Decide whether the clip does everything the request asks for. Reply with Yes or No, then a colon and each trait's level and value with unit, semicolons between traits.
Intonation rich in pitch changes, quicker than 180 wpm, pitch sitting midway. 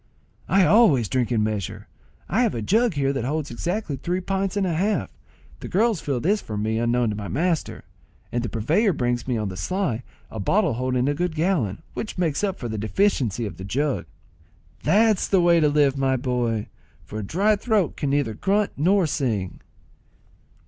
Yes: wide, 8.3 semitones; average, 195 wpm; medium, 145 Hz